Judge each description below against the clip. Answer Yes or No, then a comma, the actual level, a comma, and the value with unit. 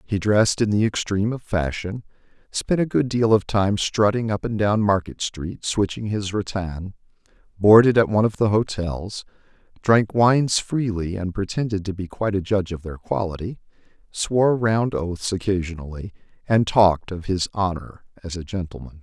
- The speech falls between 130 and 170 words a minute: Yes, average, 165 wpm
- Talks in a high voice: No, low, 100 Hz